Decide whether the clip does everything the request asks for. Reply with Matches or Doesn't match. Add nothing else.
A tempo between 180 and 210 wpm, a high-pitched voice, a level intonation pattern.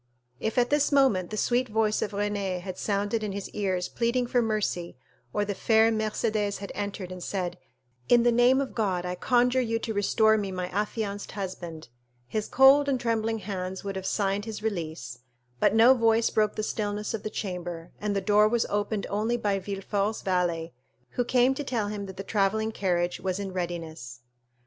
Doesn't match